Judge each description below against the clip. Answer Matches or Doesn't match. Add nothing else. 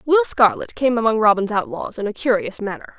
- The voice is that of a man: Doesn't match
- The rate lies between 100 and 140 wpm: Doesn't match